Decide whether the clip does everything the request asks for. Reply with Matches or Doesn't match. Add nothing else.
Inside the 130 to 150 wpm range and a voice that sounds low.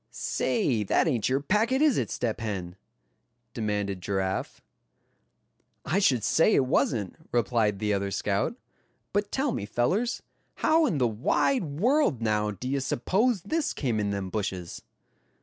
Matches